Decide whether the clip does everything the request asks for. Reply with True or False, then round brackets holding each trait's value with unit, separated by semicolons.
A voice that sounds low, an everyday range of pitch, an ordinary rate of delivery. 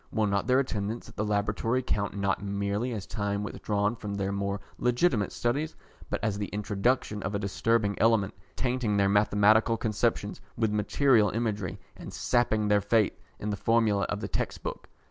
False (105 Hz; 2.2 semitones; 170 wpm)